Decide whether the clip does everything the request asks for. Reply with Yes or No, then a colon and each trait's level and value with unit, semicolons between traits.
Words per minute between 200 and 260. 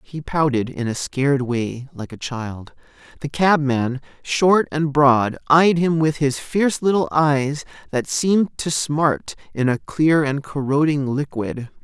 No: average, 155 wpm